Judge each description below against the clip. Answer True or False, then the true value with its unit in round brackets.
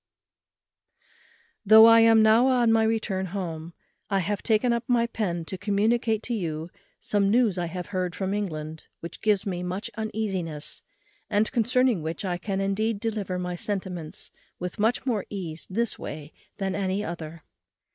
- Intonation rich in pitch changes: False (3.8 semitones)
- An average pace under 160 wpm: False (165 wpm)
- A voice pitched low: False (200 Hz)